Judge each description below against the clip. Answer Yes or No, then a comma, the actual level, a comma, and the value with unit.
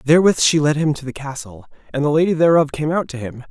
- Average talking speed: No, fast, 255 wpm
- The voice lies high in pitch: No, medium, 150 Hz